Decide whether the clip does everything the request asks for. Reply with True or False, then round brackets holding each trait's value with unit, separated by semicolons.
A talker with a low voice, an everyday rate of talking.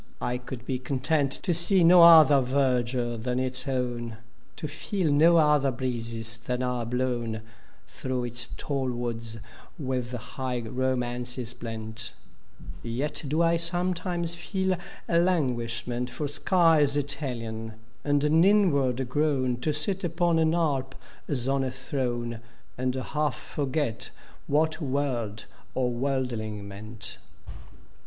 False (130 Hz; 125 wpm)